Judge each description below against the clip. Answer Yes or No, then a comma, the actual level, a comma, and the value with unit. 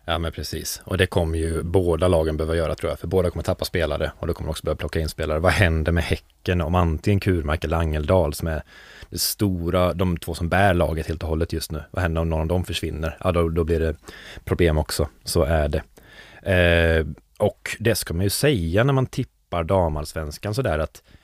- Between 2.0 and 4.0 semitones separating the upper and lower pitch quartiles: Yes, narrow, 2.5 semitones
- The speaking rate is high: Yes, fast, 225 wpm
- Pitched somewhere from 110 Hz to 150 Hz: No, very low, 85 Hz